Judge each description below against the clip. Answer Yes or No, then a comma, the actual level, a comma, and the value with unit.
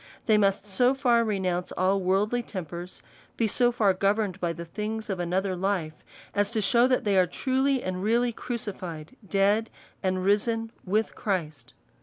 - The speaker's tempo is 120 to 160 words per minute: No, average, 170 wpm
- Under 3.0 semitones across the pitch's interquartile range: No, average, 3.5 semitones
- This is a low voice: No, high, 200 Hz